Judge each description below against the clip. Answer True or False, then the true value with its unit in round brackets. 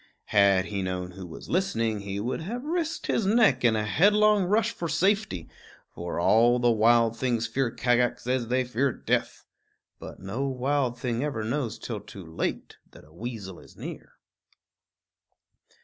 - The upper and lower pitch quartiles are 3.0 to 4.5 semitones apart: False (5.6 semitones)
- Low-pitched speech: True (120 Hz)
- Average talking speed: True (165 wpm)